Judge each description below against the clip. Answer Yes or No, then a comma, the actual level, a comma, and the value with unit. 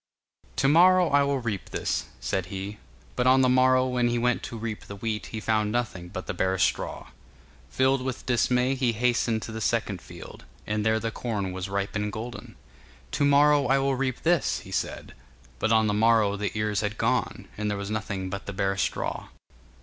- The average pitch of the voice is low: Yes, low, 110 Hz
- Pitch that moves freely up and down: No, average, 3.8 semitones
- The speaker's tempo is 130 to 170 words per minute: No, fast, 205 wpm